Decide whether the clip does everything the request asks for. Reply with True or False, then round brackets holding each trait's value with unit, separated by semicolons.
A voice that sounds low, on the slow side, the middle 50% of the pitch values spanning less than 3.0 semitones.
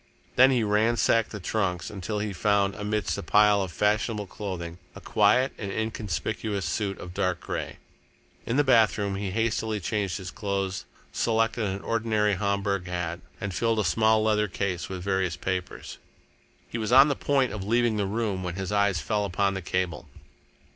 False (105 Hz; 175 wpm; 2.5 semitones)